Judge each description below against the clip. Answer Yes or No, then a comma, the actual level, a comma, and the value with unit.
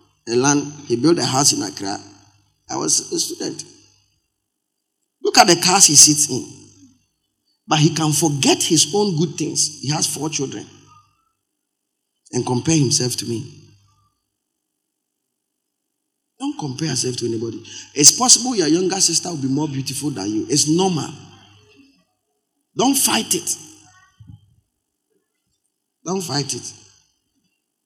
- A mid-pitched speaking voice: Yes, medium, 155 Hz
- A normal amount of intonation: No, wide, 8.3 semitones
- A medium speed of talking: No, slow, 130 wpm